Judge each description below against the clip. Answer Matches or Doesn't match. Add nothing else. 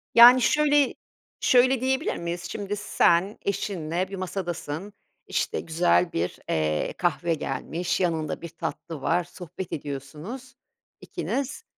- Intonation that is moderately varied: Doesn't match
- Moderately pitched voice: Matches